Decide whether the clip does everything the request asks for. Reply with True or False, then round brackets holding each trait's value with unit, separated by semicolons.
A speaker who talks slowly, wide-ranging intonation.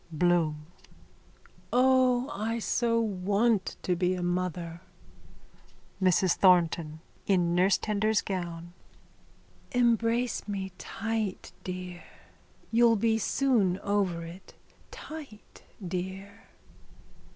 False (90 wpm; 4.2 semitones)